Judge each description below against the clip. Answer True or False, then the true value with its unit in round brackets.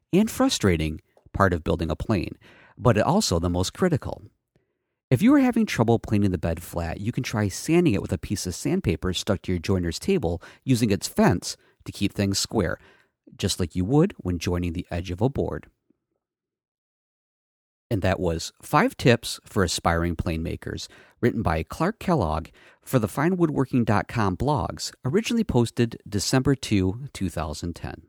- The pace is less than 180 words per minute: True (160 wpm)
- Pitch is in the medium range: False (100 Hz)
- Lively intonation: True (5.7 semitones)